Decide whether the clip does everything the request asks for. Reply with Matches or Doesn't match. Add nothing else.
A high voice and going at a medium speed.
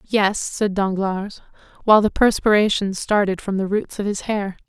Matches